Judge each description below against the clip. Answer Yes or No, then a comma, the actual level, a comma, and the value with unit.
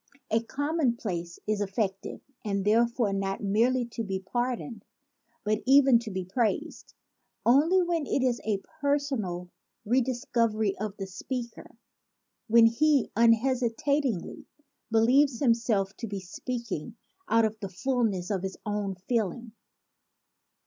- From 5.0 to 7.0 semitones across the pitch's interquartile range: No, average, 4.1 semitones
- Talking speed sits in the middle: No, slow, 130 wpm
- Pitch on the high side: Yes, high, 230 Hz